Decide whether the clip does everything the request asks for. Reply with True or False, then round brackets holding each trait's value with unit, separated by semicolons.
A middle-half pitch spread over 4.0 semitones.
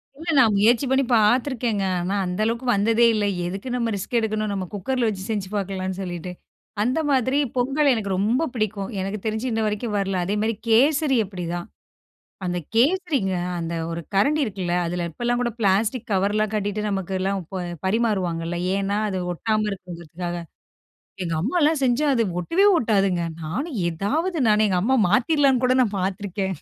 True (4.4 semitones)